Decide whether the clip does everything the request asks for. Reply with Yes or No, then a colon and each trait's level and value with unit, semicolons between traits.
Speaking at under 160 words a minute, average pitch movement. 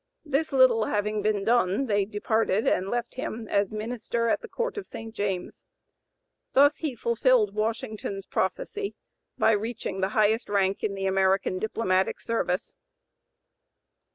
Yes: average, 140 wpm; average, 3.2 semitones